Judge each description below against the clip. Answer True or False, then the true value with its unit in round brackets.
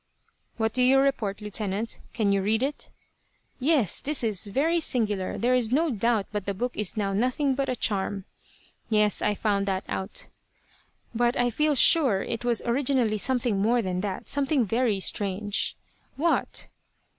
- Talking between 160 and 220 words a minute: True (165 wpm)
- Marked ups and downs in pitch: False (4.0 semitones)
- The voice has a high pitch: True (225 Hz)